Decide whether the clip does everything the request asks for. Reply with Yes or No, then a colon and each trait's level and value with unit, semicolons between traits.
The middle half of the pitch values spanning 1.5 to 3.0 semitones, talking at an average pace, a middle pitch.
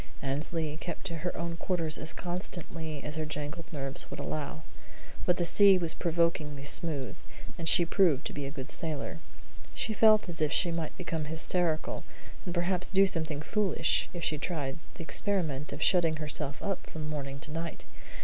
Yes: average, 2.7 semitones; average, 180 wpm; medium, 160 Hz